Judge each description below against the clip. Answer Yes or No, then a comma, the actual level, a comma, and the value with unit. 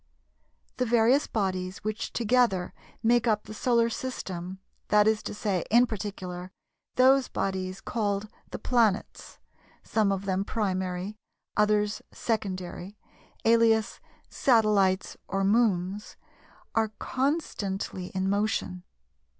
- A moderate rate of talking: No, slow, 100 wpm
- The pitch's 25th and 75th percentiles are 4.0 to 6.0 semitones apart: No, average, 3.2 semitones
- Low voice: No, high, 210 Hz